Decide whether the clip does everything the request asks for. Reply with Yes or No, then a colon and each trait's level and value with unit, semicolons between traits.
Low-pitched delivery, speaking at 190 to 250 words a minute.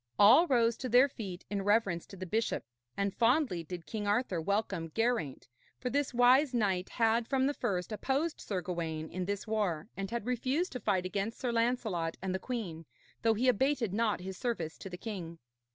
No: high, 215 Hz; average, 195 wpm